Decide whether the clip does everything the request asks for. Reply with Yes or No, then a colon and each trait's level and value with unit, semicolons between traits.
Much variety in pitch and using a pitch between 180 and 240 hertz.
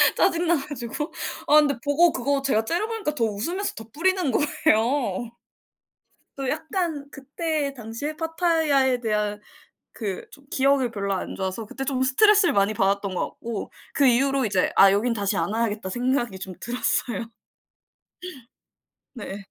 No: wide, 5.8 semitones; very high, 260 Hz